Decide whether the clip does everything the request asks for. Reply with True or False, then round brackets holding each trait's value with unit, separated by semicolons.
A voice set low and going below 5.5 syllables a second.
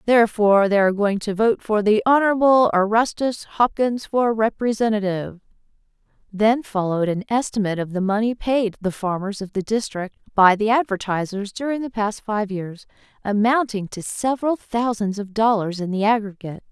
False (215 Hz; 5.3 syllables/s)